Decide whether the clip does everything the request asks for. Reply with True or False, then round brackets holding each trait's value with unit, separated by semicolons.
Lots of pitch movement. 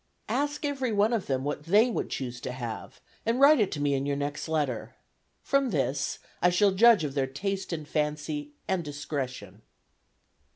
True (6.9 semitones)